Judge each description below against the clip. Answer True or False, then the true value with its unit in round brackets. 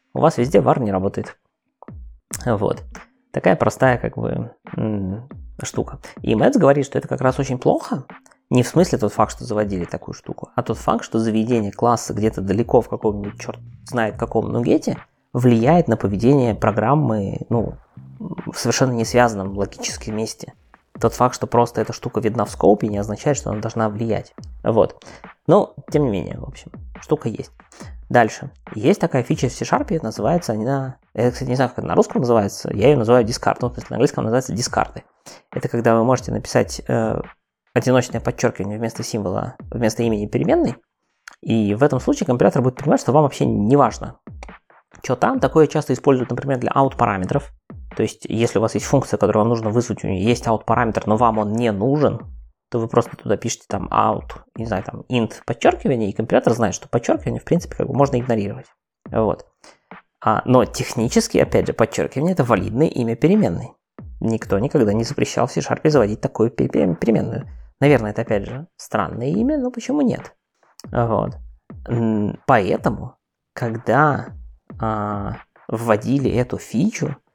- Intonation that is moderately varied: True (3.3 semitones)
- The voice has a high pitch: False (115 Hz)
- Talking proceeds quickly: True (170 wpm)